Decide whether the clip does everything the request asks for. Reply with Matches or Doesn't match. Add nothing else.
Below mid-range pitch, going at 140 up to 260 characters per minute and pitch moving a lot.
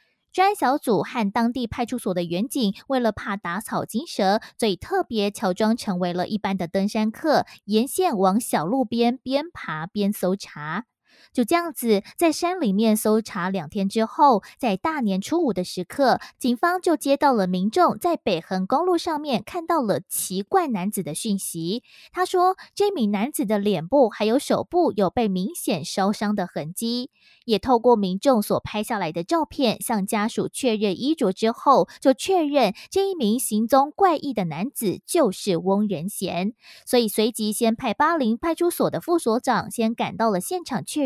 Doesn't match